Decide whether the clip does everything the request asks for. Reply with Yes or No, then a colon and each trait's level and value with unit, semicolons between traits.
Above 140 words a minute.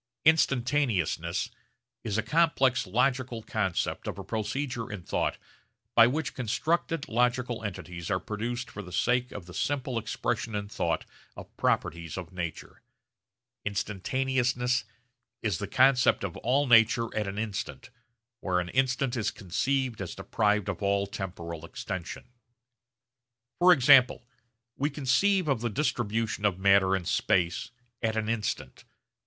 No: slow, 135 wpm